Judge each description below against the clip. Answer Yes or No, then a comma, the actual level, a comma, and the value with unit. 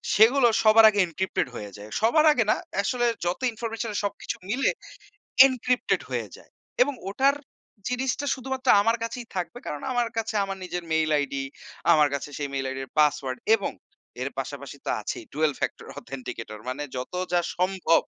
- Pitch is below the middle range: No, high, 200 Hz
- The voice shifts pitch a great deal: Yes, wide, 8.6 semitones